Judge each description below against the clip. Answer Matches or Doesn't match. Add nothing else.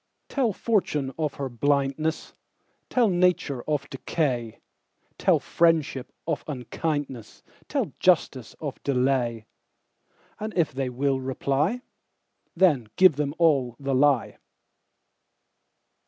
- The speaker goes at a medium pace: Doesn't match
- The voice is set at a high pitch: Doesn't match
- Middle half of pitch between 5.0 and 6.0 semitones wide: Doesn't match